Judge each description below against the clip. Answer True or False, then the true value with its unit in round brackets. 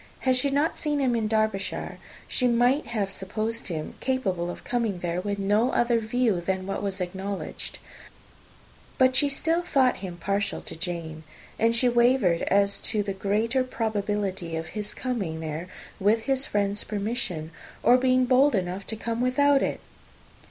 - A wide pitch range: False (4.7 semitones)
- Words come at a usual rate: True (165 wpm)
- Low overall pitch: False (215 Hz)